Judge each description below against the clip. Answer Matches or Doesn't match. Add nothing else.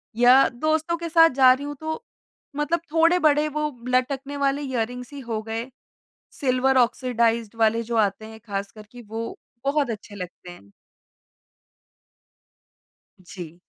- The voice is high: Matches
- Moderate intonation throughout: Matches